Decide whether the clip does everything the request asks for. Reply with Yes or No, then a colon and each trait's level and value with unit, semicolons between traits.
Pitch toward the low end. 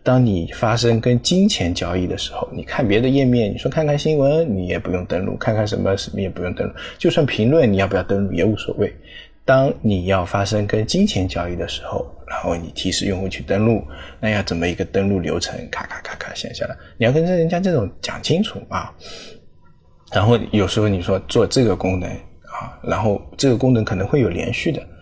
Yes: low, 105 Hz